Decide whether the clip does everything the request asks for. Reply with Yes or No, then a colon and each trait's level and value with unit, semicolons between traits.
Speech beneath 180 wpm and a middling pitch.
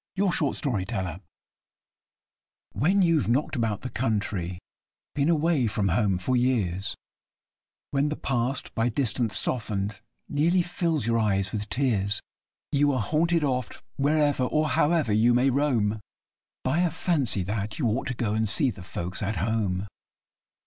No: average, 150 wpm; low, 120 Hz